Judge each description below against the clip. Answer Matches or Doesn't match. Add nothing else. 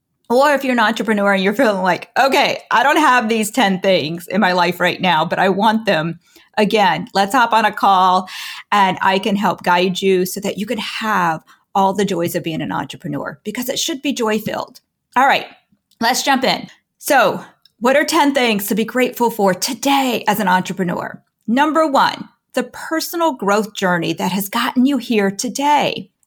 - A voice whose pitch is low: Doesn't match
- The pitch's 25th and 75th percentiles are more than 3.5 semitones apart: Matches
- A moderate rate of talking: Matches